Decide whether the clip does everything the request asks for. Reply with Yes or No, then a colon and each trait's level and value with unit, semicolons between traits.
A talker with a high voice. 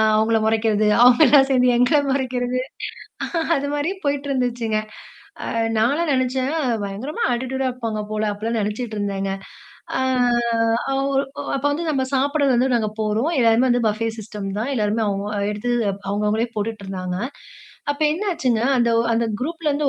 Yes: high, 245 Hz